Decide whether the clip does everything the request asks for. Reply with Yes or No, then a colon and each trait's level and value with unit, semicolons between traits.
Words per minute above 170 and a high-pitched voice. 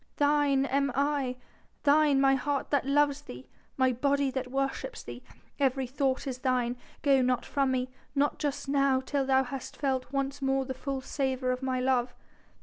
Yes: average, 180 wpm; very high, 270 Hz